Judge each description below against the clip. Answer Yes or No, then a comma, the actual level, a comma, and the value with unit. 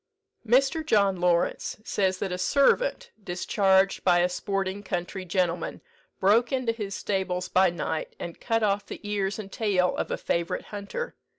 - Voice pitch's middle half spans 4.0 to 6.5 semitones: No, average, 2.9 semitones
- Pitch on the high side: Yes, high, 195 Hz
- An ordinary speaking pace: Yes, average, 160 wpm